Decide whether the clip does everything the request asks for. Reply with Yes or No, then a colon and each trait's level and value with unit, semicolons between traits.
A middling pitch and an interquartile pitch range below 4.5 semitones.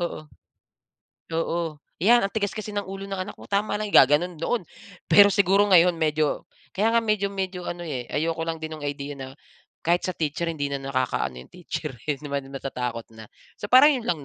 No: medium, 170 Hz; wide, 5.6 semitones